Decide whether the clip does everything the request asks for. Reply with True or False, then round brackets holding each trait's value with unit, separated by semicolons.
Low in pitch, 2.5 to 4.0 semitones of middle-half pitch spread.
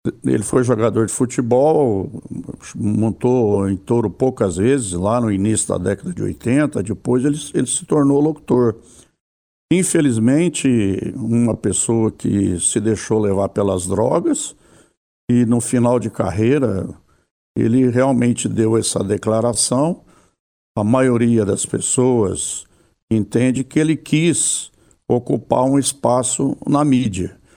True (120 Hz; 3.6 semitones)